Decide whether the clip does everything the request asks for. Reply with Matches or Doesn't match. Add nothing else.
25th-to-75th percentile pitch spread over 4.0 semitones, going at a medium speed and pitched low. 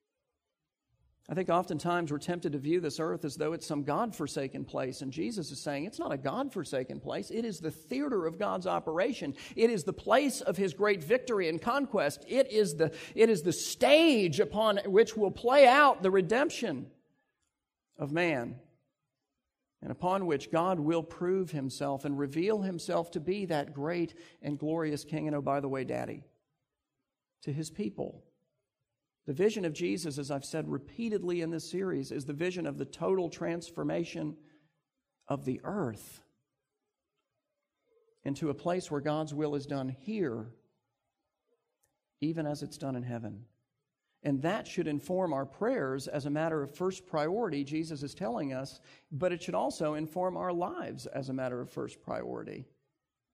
Doesn't match